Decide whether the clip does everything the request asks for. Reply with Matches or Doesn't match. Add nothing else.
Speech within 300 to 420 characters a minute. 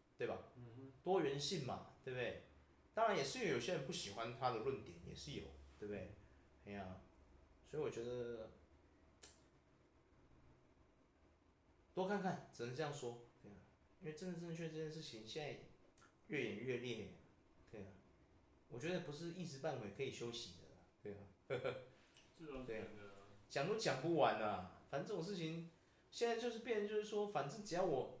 Doesn't match